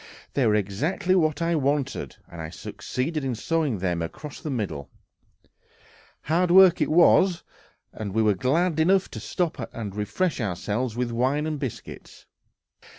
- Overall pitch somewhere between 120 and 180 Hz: Yes, low, 135 Hz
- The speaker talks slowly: No, average, 150 wpm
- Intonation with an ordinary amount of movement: No, wide, 7.4 semitones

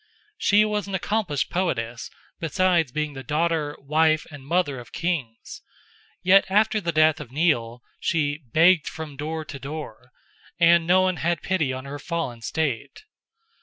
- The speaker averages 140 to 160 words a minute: Yes, average, 155 wpm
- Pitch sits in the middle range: Yes, medium, 155 Hz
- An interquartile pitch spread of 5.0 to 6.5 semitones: No, average, 4.0 semitones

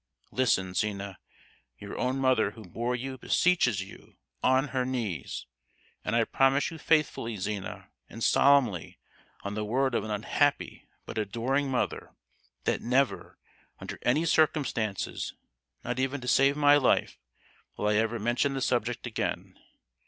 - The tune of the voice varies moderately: Yes, average, 4.0 semitones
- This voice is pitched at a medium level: No, low, 125 Hz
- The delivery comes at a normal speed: Yes, average, 145 wpm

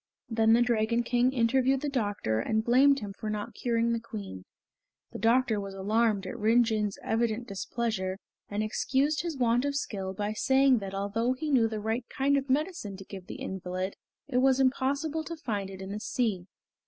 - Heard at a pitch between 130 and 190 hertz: No, high, 230 Hz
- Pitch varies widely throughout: No, average, 4.2 semitones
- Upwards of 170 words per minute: Yes, average, 190 wpm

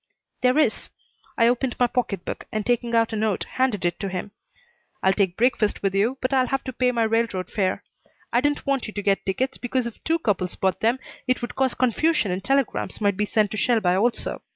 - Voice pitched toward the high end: Yes, high, 230 Hz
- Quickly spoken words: Yes, fast, 225 wpm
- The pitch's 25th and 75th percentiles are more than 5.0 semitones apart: No, average, 4.0 semitones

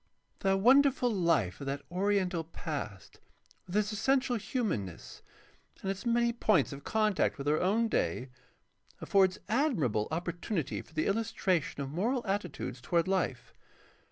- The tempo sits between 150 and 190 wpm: No, slow, 135 wpm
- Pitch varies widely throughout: Yes, wide, 6.4 semitones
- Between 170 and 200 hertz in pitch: Yes, high, 190 Hz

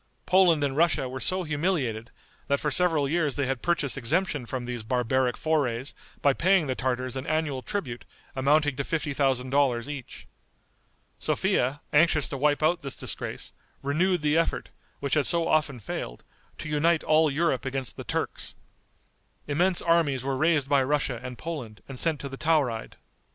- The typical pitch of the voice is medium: Yes, medium, 145 Hz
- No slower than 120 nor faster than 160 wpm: No, average, 170 wpm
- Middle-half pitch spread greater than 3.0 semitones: Yes, average, 3.5 semitones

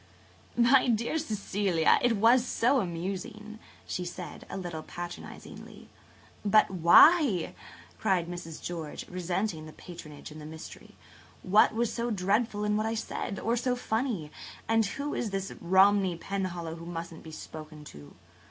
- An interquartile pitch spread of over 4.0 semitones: Yes, average, 4.7 semitones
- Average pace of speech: Yes, average, 150 wpm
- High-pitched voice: Yes, high, 195 Hz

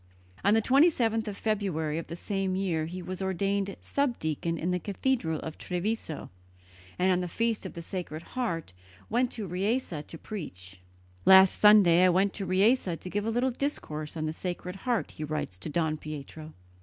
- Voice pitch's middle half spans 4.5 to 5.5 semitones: Yes, average, 4.8 semitones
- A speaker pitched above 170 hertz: Yes, medium, 185 Hz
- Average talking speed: Yes, average, 180 wpm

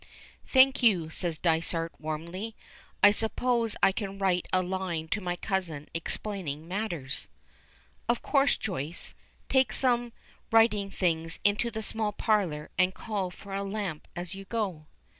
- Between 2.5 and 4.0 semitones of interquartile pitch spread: No, average, 4.6 semitones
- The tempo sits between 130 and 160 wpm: Yes, average, 140 wpm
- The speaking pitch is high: Yes, high, 195 Hz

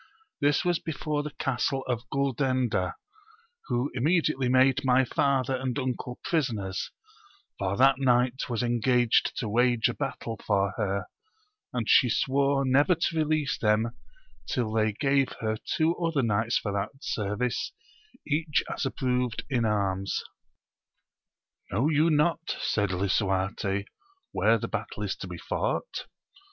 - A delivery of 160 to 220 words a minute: No, average, 140 wpm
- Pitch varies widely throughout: No, average, 4.2 semitones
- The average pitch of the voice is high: No, low, 125 Hz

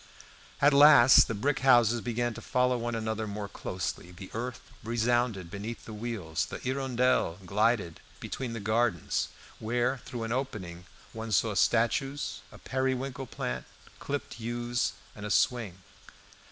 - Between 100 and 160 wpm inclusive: Yes, average, 140 wpm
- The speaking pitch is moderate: No, low, 115 Hz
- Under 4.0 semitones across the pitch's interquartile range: Yes, average, 3.2 semitones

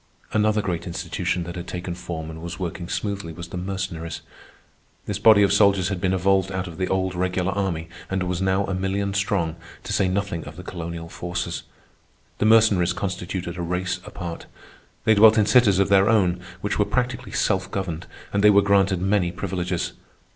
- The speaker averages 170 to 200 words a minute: Yes, average, 190 wpm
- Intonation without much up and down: Yes, narrow, 2.3 semitones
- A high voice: No, very low, 95 Hz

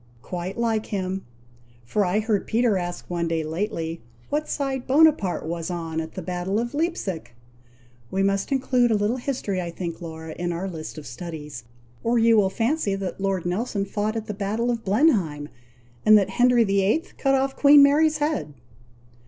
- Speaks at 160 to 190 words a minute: Yes, average, 175 wpm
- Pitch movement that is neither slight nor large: No, wide, 5.7 semitones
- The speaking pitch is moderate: No, high, 200 Hz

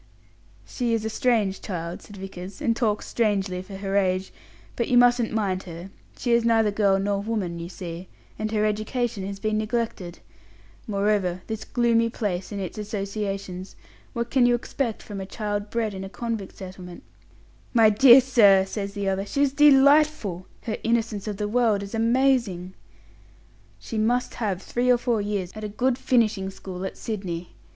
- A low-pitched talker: No, high, 210 Hz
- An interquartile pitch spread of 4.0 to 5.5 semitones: No, average, 3.3 semitones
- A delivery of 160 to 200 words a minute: Yes, average, 175 wpm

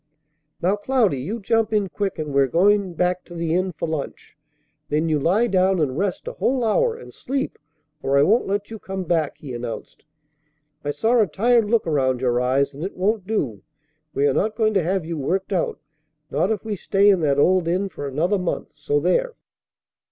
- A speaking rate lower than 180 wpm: No, fast, 205 wpm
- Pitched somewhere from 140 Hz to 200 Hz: Yes, medium, 185 Hz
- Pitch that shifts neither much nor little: No, wide, 5.8 semitones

